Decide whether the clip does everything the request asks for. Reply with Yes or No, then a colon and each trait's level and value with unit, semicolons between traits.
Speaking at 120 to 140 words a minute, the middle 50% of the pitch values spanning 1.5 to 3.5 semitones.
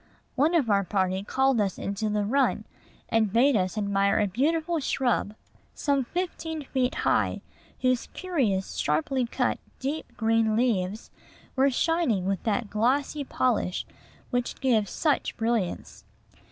No: slow, 135 wpm; average, 5.3 semitones